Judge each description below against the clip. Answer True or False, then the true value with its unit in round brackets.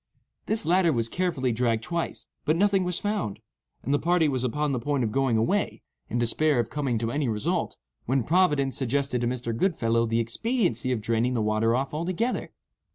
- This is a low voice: True (130 Hz)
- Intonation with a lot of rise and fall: True (6.2 semitones)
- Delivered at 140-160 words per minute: False (190 wpm)